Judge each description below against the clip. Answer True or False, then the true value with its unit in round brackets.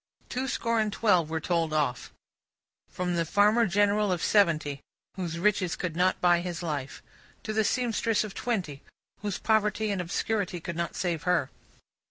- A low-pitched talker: False (180 Hz)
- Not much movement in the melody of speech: False (4.0 semitones)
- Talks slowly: False (165 wpm)